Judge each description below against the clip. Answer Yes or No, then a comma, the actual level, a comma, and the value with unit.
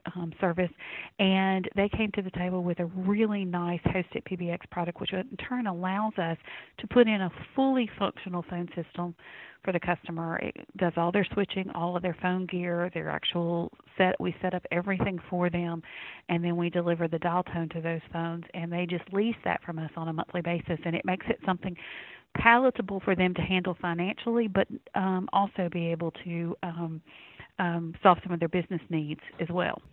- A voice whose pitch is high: No, medium, 180 Hz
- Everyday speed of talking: Yes, average, 195 wpm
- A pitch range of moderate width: No, narrow, 1.9 semitones